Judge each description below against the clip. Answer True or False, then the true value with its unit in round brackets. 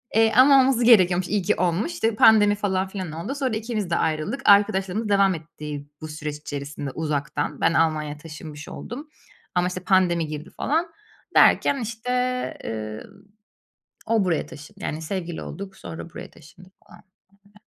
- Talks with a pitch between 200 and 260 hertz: False (185 Hz)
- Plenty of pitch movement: True (5.8 semitones)